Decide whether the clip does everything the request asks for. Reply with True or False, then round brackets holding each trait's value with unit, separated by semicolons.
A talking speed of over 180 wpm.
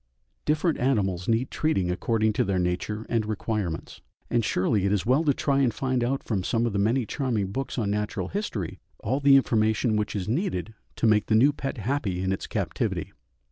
True (200 wpm)